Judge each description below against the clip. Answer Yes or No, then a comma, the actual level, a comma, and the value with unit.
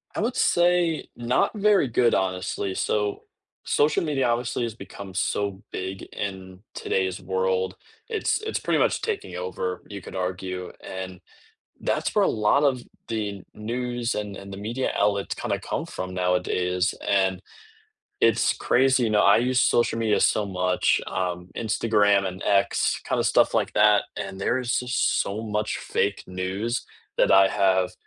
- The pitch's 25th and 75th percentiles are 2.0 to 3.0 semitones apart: No, average, 4.1 semitones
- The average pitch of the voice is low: Yes, low, 100 Hz